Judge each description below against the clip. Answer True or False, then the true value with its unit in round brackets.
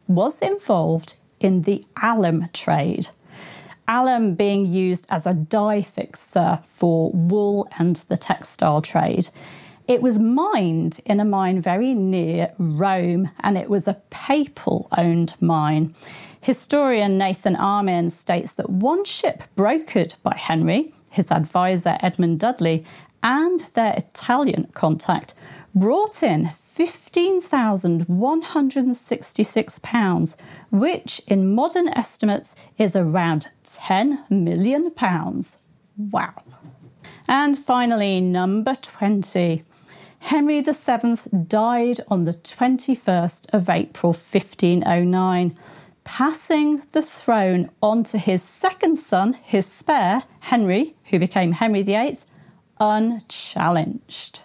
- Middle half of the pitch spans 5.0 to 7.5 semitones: True (5.6 semitones)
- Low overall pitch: False (200 Hz)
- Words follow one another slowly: True (105 wpm)